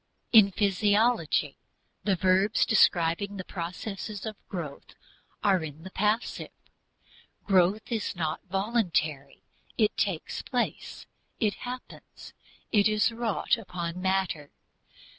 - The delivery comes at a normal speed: No, slow, 105 wpm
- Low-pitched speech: No, high, 195 Hz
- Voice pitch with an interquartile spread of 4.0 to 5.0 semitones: No, average, 3.6 semitones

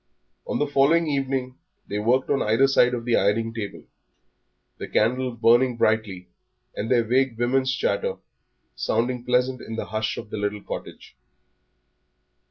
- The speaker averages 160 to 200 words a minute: No, average, 150 wpm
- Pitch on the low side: Yes, low, 120 Hz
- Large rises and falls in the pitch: No, average, 3.0 semitones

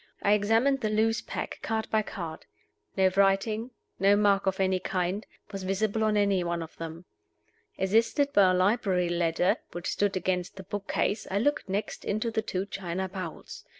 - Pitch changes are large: No, average, 2.7 semitones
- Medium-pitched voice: No, high, 195 Hz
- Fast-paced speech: No, average, 180 wpm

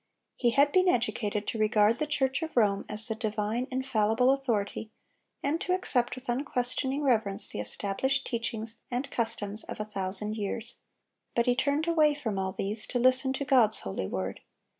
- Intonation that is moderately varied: Yes, average, 4.0 semitones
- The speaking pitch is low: No, high, 235 Hz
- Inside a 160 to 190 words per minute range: Yes, average, 175 wpm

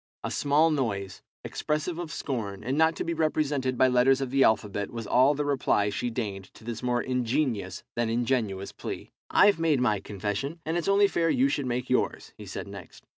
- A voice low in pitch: Yes, low, 130 Hz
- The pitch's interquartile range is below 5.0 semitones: No, average, 5.3 semitones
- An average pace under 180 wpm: No, average, 200 wpm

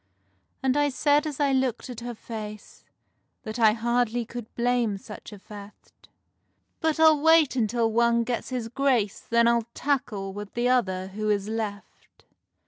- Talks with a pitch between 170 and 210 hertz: No, high, 235 Hz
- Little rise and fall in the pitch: No, average, 3.2 semitones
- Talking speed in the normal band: Yes, average, 160 wpm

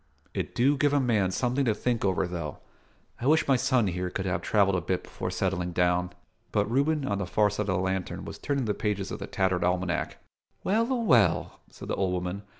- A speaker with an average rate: No, fast, 225 wpm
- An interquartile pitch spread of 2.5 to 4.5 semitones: No, wide, 5.5 semitones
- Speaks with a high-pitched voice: No, low, 100 Hz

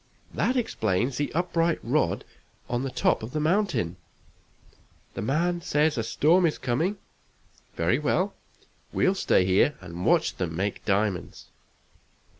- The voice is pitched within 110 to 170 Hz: Yes, low, 135 Hz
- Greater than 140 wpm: No, slow, 135 wpm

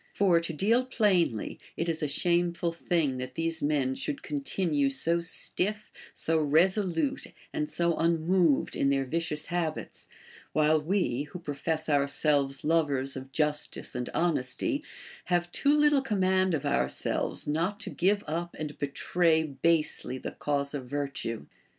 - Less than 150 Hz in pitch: No, medium, 165 Hz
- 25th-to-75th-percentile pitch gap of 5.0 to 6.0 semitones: No, average, 3.8 semitones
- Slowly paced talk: No, average, 145 wpm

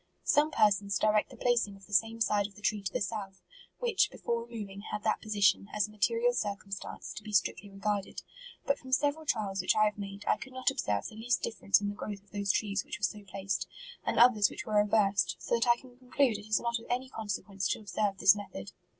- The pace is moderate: No, fast, 240 wpm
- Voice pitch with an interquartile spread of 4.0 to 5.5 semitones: No, average, 2.8 semitones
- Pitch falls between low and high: No, high, 210 Hz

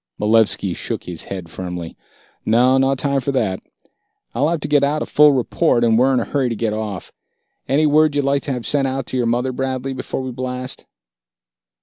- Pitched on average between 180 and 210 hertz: No, low, 130 Hz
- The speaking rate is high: Yes, fast, 210 wpm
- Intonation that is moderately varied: Yes, average, 3.5 semitones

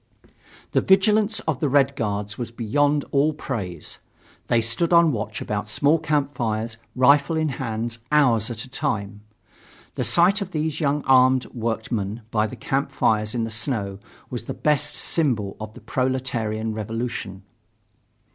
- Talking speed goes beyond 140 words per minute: Yes, average, 155 wpm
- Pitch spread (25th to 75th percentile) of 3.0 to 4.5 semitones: No, average, 5.0 semitones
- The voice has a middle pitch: No, low, 125 Hz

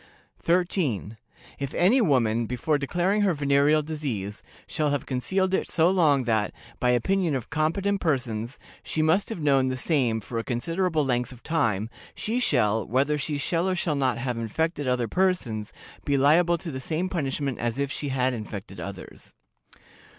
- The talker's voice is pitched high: No, medium, 140 Hz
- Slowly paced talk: No, average, 170 wpm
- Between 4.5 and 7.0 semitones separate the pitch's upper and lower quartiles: Yes, wide, 5.4 semitones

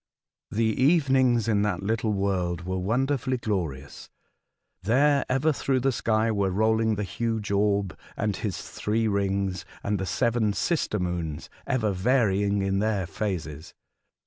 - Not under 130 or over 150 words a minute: Yes, average, 140 wpm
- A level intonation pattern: No, average, 3.4 semitones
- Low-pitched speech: Yes, low, 105 Hz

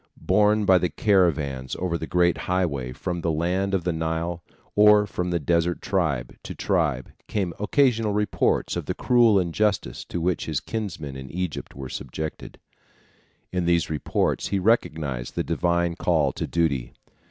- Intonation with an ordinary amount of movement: Yes, average, 3.7 semitones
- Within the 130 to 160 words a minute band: Yes, average, 155 wpm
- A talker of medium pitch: No, very low, 85 Hz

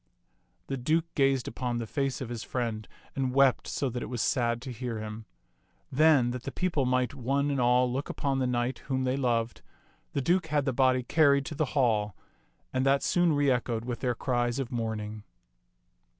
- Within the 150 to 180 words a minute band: No, average, 195 wpm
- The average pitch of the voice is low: Yes, low, 125 Hz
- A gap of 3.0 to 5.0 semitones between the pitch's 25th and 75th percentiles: No, narrow, 2.4 semitones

